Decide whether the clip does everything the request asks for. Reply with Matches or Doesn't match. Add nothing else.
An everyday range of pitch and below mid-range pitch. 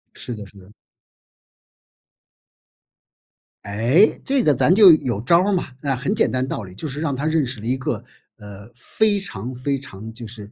Doesn't match